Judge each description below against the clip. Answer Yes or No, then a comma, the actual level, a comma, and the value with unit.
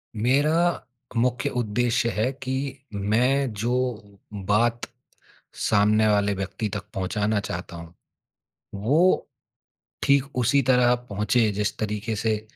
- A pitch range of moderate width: Yes, average, 3.3 semitones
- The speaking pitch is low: Yes, low, 110 Hz